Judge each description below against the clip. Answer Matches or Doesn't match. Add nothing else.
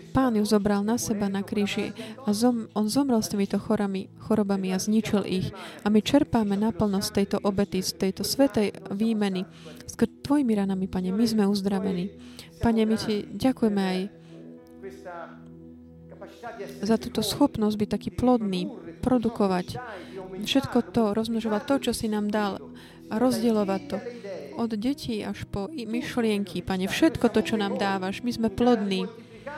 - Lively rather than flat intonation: Doesn't match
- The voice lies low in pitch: Doesn't match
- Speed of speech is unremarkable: Matches